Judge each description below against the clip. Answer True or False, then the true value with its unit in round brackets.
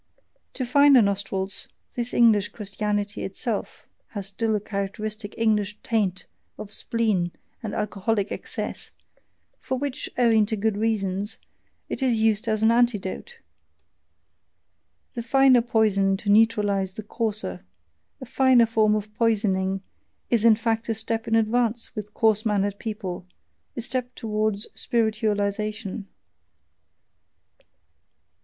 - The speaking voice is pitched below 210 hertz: False (215 Hz)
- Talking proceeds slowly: True (120 wpm)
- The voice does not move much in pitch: True (2.1 semitones)